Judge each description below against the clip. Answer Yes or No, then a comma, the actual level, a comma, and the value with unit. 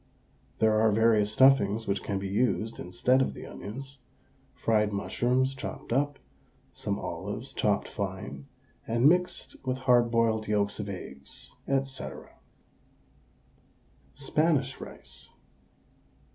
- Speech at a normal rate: No, slow, 115 wpm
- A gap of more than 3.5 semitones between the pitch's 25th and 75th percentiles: Yes, average, 4.3 semitones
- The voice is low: Yes, low, 115 Hz